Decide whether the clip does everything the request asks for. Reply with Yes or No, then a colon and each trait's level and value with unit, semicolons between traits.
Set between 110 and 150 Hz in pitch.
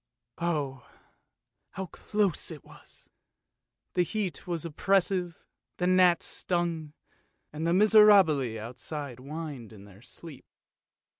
No: medium, 165 Hz